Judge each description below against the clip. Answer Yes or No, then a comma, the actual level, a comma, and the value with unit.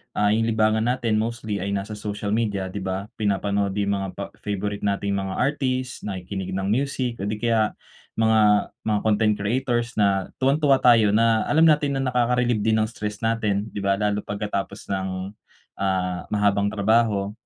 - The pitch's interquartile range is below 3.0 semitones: Yes, narrow, 2.5 semitones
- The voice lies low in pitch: Yes, low, 105 Hz